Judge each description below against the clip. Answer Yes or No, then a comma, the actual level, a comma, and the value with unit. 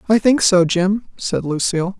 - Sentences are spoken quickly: No, average, 180 wpm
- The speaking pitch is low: No, high, 190 Hz